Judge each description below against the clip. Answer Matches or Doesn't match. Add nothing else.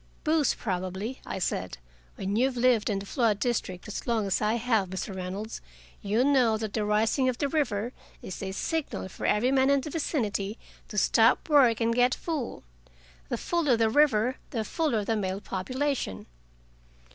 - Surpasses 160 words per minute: Matches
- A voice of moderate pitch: Doesn't match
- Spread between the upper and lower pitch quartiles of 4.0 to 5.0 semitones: Matches